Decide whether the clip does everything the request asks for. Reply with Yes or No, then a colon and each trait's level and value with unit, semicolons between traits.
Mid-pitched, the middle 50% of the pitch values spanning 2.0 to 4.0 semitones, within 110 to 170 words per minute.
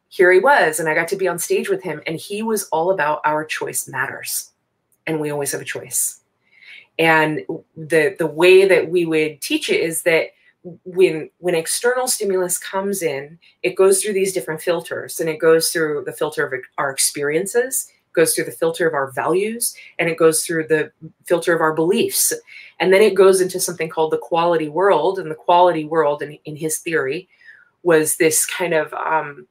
No: medium, 170 Hz; average, 3.2 semitones; average, 195 wpm